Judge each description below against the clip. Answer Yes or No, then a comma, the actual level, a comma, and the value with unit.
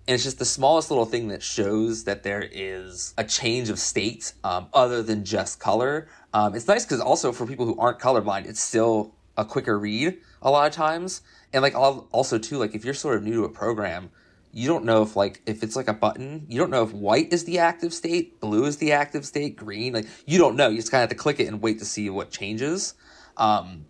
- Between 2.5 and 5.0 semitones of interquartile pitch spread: No, wide, 5.4 semitones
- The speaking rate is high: Yes, fast, 245 wpm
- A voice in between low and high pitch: No, low, 115 Hz